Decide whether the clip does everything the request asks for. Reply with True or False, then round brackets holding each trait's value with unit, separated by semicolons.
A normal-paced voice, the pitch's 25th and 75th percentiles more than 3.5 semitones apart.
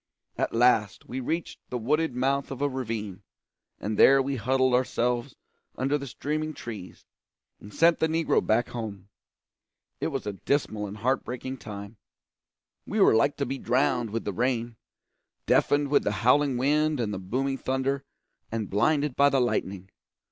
True (165 wpm; 4.1 semitones)